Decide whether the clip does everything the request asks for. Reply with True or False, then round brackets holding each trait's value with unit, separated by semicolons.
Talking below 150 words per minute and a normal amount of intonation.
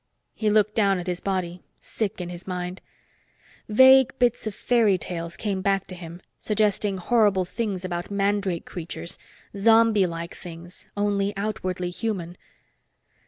True (140 wpm; 3.0 semitones)